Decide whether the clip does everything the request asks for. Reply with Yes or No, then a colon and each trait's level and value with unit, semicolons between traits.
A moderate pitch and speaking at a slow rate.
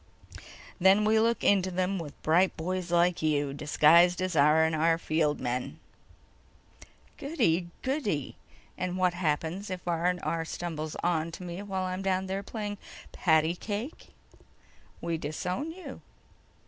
Yes: medium, 175 Hz; slow, 120 wpm